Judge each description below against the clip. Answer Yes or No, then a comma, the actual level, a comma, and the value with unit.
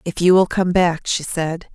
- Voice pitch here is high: No, medium, 175 Hz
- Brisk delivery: Yes, fast, 240 wpm